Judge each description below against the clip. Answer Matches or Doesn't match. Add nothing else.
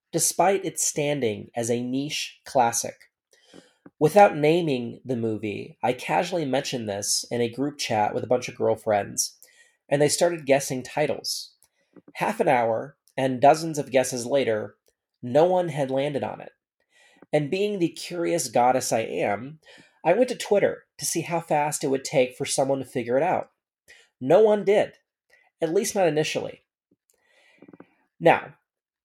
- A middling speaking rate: Matches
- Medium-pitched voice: Matches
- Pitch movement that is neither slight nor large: Matches